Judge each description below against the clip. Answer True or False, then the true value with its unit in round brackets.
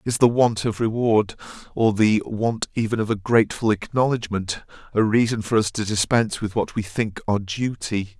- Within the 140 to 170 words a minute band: False (185 wpm)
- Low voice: True (110 Hz)